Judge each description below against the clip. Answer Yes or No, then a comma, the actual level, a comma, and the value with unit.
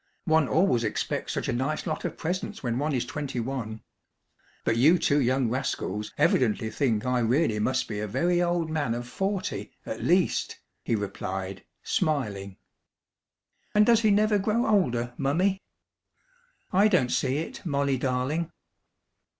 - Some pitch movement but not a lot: No, wide, 6.6 semitones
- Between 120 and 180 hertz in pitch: Yes, low, 135 Hz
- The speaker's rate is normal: Yes, average, 150 wpm